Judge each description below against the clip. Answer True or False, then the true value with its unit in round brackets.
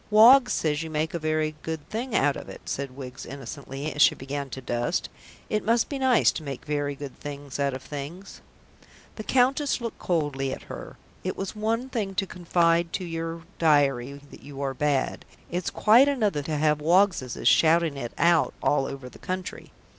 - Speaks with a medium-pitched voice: True (155 Hz)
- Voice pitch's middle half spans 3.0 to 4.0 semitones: False (5.6 semitones)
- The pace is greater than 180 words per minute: True (190 wpm)